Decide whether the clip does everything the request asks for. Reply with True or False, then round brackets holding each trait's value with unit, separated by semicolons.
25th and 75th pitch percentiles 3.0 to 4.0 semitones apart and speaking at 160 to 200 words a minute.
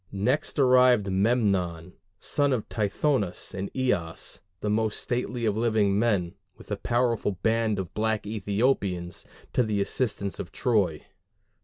False (3.7 semitones; 135 wpm)